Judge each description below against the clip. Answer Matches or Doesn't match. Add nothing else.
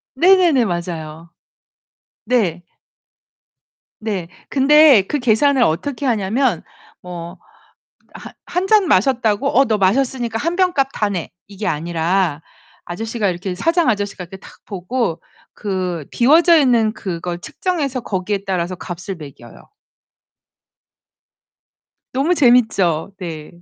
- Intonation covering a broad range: Matches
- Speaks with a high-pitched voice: Matches